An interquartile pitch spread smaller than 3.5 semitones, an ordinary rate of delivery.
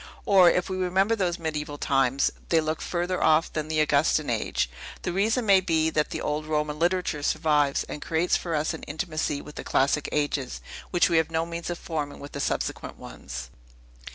Yes: average, 2.8 semitones; average, 195 wpm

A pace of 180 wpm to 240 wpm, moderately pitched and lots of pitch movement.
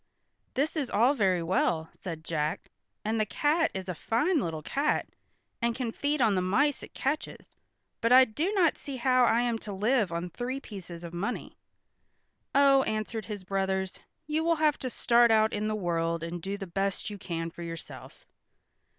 No: average, 185 wpm; high, 215 Hz; wide, 6.5 semitones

